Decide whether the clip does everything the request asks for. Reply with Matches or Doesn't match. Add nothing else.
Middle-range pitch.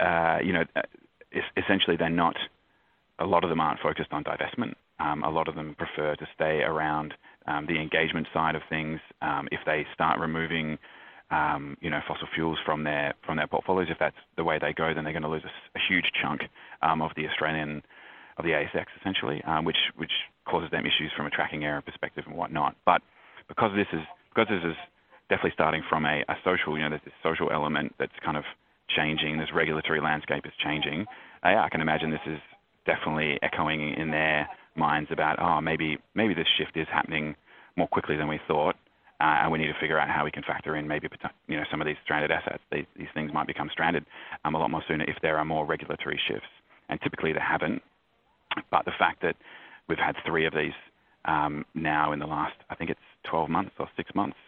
Doesn't match